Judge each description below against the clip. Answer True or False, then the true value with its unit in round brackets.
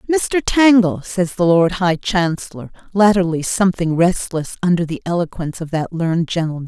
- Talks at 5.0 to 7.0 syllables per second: True (5.1 syllables/s)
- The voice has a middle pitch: True (175 Hz)